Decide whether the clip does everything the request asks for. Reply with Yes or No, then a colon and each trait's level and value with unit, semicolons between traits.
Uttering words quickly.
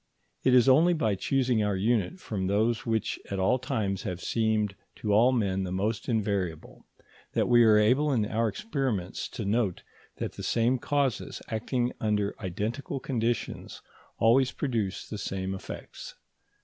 No: average, 155 wpm